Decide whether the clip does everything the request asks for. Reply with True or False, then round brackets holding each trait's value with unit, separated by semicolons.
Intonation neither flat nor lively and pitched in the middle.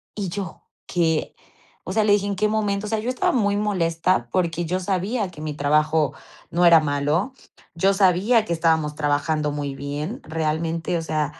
True (4.6 semitones; 170 Hz)